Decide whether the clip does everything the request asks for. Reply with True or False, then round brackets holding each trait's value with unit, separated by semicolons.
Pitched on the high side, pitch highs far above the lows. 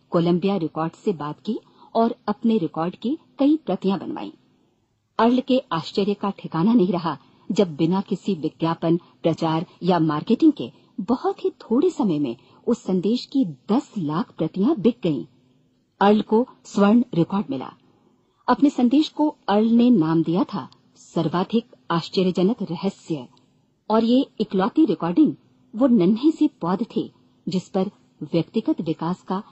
True (195 Hz; 6.1 semitones)